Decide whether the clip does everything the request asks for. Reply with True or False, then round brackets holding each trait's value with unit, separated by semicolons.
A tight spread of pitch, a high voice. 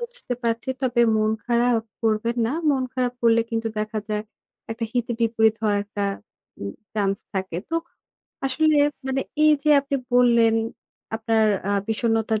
True (2.3 semitones; 230 Hz)